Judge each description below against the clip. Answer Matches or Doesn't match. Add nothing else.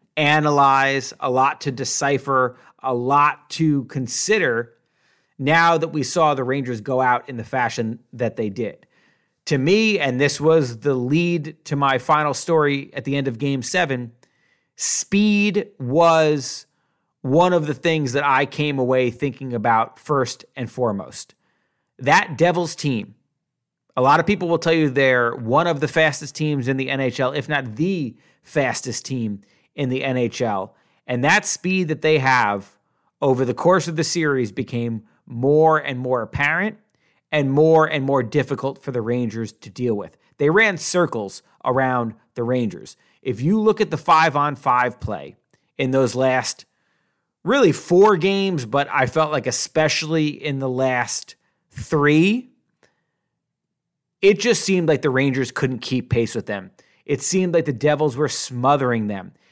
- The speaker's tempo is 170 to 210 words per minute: Doesn't match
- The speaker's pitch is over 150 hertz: Doesn't match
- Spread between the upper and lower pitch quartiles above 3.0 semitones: Matches